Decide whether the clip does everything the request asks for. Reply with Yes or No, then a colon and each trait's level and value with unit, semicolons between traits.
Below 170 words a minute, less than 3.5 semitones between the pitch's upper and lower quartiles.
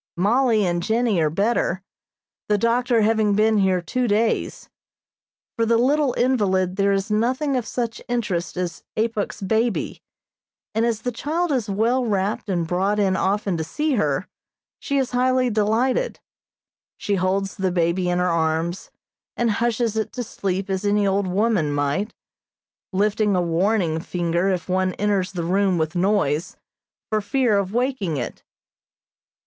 No: average, 155 wpm; average, 4.1 semitones